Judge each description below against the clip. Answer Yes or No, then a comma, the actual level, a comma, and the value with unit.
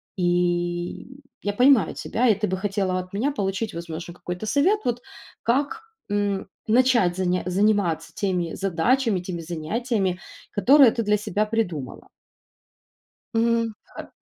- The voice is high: Yes, high, 205 Hz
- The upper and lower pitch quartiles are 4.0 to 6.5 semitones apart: Yes, average, 4.6 semitones